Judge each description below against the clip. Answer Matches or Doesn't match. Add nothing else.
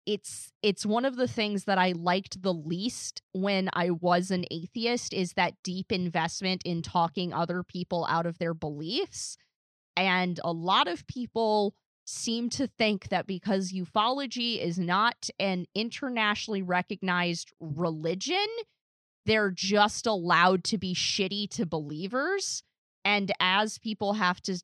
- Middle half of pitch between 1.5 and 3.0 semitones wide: Doesn't match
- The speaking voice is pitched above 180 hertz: Matches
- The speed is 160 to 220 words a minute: Doesn't match